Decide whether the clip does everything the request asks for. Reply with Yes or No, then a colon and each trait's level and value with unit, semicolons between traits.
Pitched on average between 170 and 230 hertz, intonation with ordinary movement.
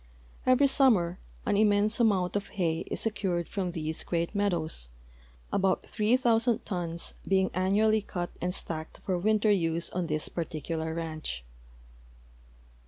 Yes: medium, 185 Hz; average, 4.0 semitones